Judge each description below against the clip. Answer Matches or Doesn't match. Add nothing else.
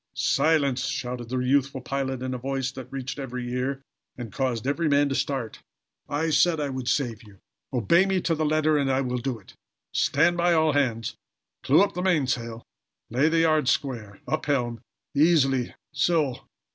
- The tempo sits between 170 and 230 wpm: Matches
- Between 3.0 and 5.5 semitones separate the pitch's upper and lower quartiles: Matches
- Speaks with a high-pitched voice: Doesn't match